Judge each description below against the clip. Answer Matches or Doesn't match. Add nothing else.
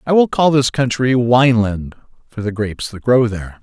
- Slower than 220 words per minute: Matches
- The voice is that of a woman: Doesn't match